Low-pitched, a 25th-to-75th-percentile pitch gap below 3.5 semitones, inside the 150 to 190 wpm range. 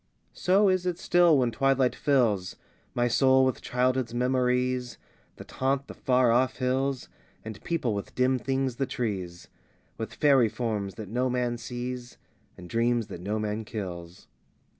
Yes: low, 125 Hz; average, 2.9 semitones; average, 160 wpm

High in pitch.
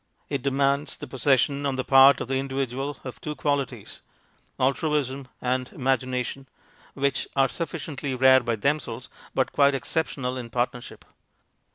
No: low, 135 Hz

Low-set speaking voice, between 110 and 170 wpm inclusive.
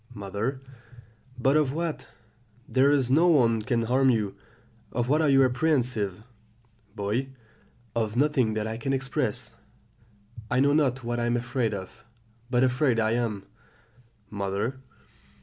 Yes: low, 125 Hz; average, 140 wpm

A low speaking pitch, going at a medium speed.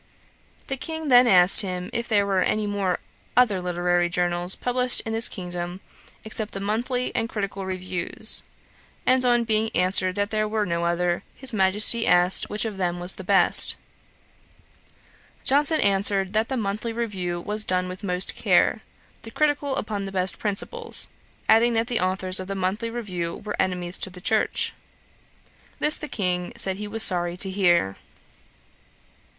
No: high, 200 Hz; average, 160 wpm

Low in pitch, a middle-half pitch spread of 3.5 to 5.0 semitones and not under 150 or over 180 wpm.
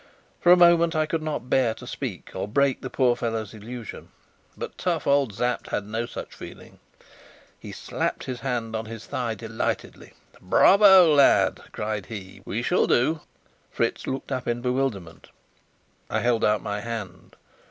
Yes: low, 120 Hz; average, 4.2 semitones; average, 165 wpm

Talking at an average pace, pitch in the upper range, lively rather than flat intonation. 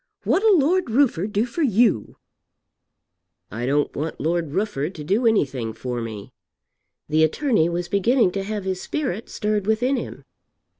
Yes: average, 150 wpm; high, 195 Hz; wide, 7.4 semitones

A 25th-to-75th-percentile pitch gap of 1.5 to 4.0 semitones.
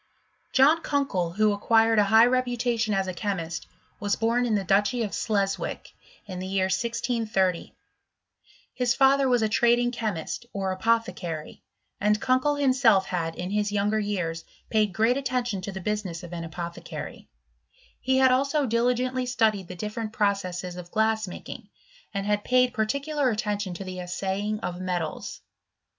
No: average, 4.4 semitones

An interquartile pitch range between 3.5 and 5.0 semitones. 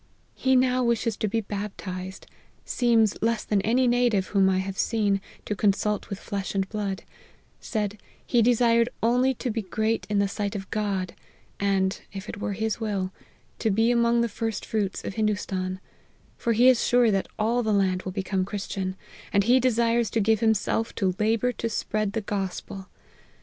No: average, 2.8 semitones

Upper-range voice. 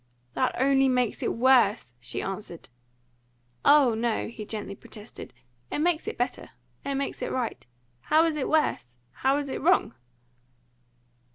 Yes: very high, 255 Hz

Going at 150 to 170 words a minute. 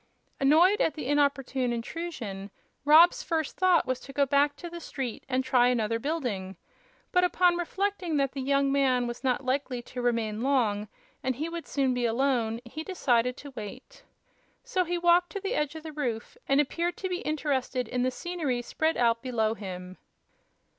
No: average, 180 wpm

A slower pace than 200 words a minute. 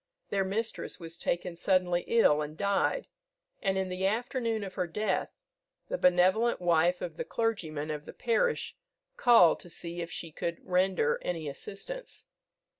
Yes: average, 155 wpm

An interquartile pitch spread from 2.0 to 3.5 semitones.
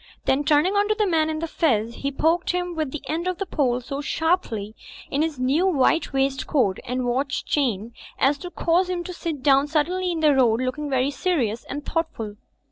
No: average, 4.5 semitones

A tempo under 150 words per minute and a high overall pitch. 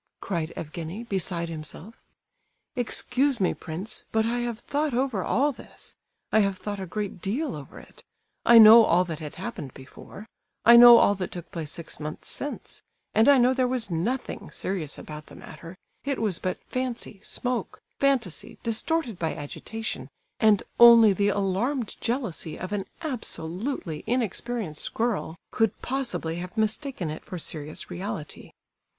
No: average, 155 wpm; high, 210 Hz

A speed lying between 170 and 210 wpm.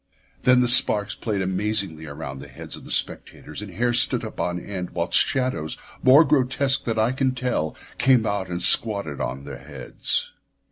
Yes: average, 180 wpm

